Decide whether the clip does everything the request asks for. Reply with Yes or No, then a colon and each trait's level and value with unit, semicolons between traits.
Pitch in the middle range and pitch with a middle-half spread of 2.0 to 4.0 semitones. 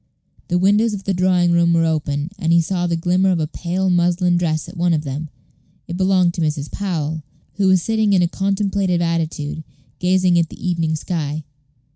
Yes: medium, 175 Hz; narrow, 2.6 semitones